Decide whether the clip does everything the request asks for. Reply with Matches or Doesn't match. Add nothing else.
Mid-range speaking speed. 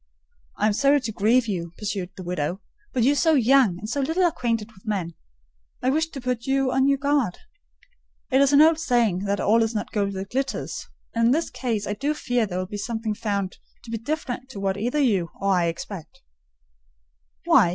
Doesn't match